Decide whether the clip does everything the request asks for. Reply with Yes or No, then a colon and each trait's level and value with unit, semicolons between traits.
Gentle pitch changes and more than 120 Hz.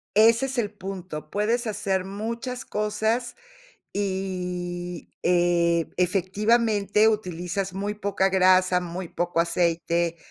No: average, 3.1 semitones; high, 190 Hz